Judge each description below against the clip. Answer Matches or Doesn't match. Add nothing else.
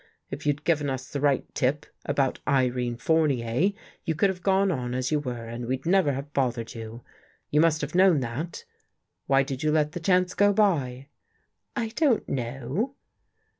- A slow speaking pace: Doesn't match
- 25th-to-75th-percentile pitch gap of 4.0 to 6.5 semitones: Matches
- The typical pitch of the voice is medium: Matches